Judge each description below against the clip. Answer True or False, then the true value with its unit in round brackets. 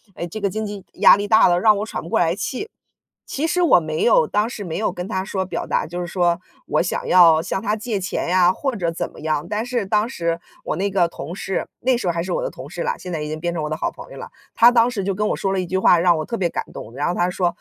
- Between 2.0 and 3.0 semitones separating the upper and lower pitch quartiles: False (3.8 semitones)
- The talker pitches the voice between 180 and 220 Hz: True (185 Hz)